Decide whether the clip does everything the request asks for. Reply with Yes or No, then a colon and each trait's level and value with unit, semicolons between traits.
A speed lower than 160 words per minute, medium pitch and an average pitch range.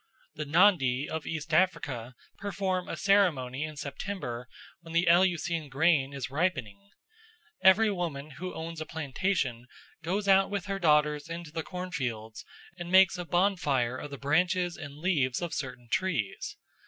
Yes: average, 150 wpm; medium, 160 Hz; average, 4.9 semitones